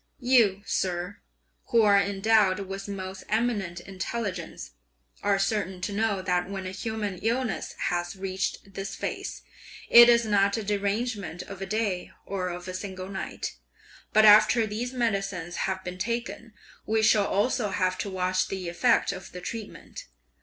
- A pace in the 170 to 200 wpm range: No, average, 155 wpm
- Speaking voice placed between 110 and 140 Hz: No, high, 200 Hz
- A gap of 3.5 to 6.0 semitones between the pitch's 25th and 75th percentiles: No, average, 2.8 semitones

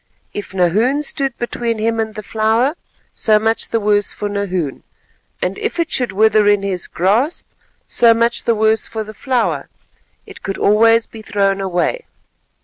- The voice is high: Yes, high, 220 Hz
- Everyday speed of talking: Yes, average, 165 wpm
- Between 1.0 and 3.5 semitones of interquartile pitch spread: Yes, narrow, 2.4 semitones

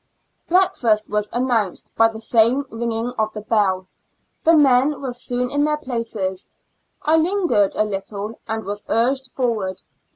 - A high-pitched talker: Yes, high, 230 Hz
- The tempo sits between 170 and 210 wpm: No, average, 155 wpm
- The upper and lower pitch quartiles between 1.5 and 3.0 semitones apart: No, average, 4.0 semitones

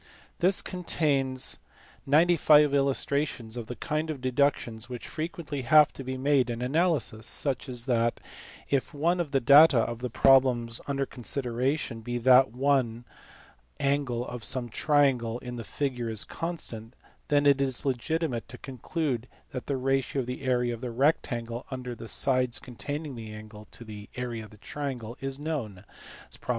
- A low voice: Yes, low, 130 Hz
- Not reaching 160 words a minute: No, average, 165 wpm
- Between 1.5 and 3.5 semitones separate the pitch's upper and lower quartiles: Yes, average, 3.2 semitones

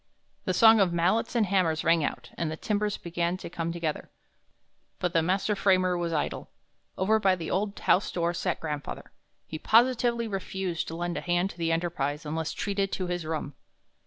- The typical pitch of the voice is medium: Yes, medium, 175 Hz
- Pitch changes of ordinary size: Yes, average, 3.1 semitones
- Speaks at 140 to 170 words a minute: No, average, 190 wpm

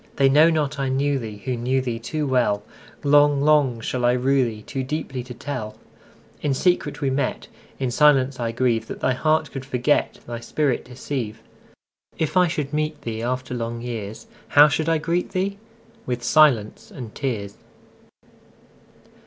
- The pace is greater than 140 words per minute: No, slow, 135 wpm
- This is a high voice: No, low, 130 Hz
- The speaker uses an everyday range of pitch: Yes, average, 3.8 semitones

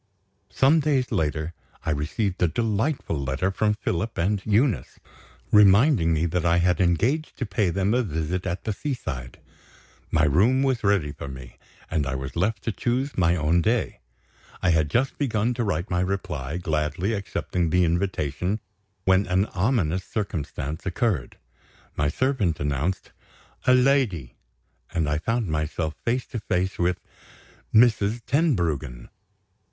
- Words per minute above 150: No, average, 145 wpm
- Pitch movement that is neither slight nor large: No, wide, 6.1 semitones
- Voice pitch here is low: Yes, very low, 90 Hz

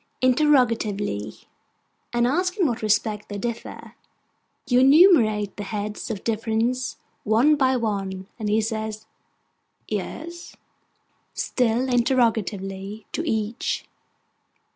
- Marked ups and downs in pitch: No, average, 3.5 semitones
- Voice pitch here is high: Yes, high, 225 Hz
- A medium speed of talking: No, slow, 100 wpm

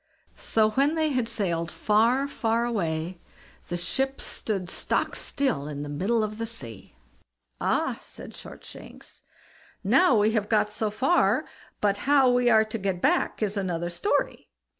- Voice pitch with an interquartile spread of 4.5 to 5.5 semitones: Yes, average, 5.2 semitones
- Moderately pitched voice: No, high, 215 Hz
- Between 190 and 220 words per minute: No, average, 155 wpm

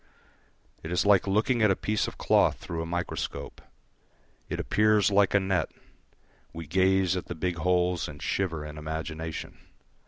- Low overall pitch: Yes, very low, 90 Hz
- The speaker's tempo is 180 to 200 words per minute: No, average, 160 wpm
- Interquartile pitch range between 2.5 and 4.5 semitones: Yes, average, 3.2 semitones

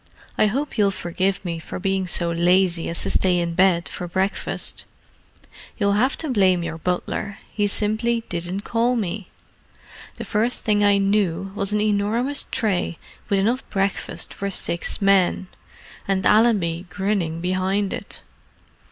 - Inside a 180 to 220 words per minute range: No, average, 145 wpm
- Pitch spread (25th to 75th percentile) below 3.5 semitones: Yes, average, 2.8 semitones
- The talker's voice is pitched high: Yes, high, 195 Hz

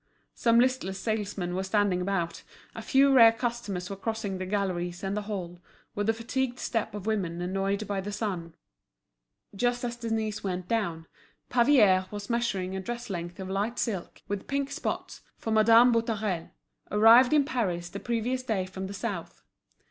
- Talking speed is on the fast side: No, average, 170 wpm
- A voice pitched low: No, high, 205 Hz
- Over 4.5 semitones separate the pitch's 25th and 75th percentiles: No, average, 3.7 semitones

